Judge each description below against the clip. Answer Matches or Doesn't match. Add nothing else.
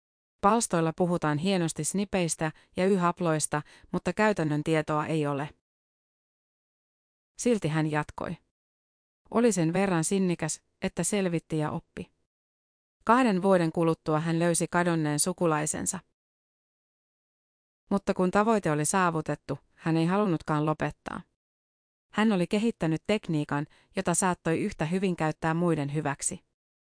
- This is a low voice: Doesn't match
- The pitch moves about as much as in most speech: Matches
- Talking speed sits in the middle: Matches